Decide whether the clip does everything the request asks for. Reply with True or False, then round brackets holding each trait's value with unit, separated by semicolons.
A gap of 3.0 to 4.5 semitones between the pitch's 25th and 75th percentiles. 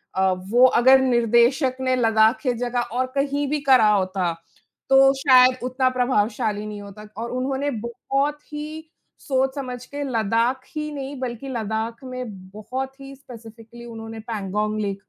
True (3.4 semitones)